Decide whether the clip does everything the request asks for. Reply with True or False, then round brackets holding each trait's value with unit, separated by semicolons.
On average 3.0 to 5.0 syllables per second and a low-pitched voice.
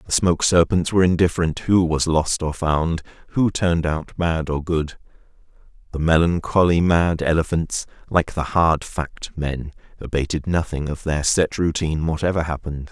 True (4.9 syllables/s; 80 Hz)